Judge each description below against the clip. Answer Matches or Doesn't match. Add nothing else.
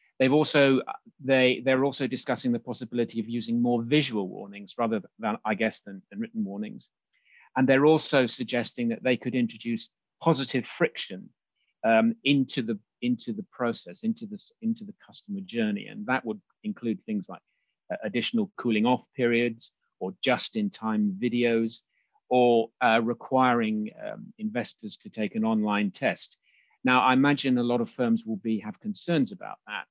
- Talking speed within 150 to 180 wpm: Matches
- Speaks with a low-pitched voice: Matches